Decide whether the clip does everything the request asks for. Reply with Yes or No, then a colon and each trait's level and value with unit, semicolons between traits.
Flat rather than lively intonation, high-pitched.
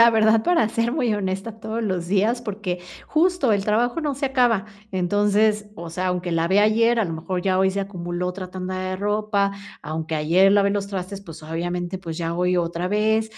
No: average, 3.4 semitones; high, 195 Hz